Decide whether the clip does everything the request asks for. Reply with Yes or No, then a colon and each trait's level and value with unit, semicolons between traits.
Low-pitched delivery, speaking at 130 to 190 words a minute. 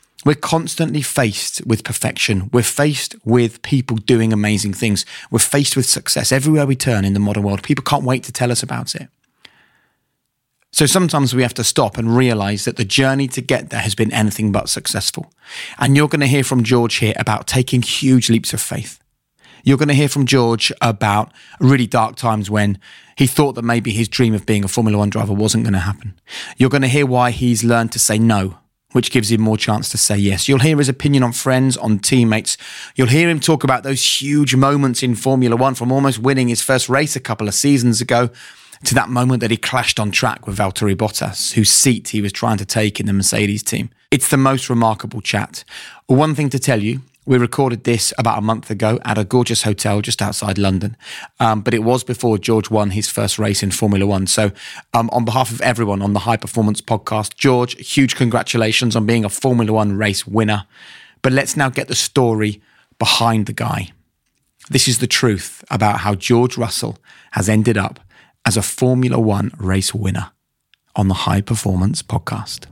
No: low, 115 Hz; fast, 205 wpm